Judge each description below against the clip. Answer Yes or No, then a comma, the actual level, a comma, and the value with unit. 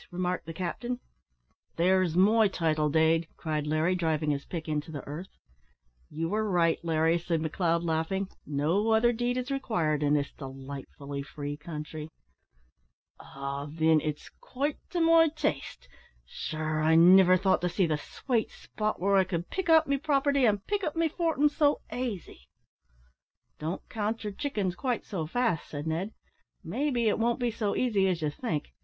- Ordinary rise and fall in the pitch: No, wide, 6.8 semitones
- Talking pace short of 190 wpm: Yes, average, 170 wpm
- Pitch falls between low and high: Yes, medium, 180 Hz